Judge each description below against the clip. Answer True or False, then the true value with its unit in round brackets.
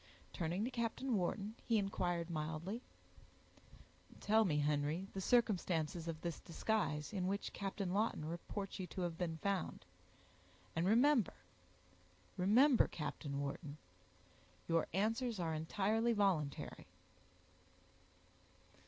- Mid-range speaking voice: True (180 Hz)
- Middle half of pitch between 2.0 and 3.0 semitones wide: False (5.2 semitones)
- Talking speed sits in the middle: False (100 wpm)